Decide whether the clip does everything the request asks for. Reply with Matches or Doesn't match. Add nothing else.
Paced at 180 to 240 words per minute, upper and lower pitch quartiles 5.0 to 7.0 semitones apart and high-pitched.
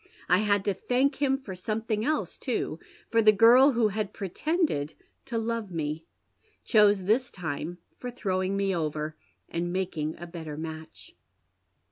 Doesn't match